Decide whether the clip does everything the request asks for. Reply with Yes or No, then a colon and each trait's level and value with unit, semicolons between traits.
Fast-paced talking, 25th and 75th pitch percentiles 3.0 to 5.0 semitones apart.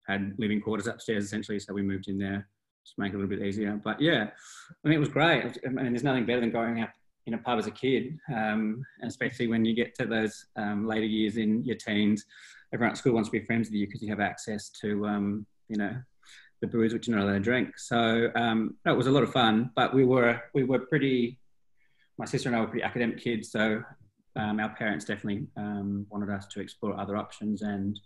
No: fast, 245 wpm; narrow, 2.6 semitones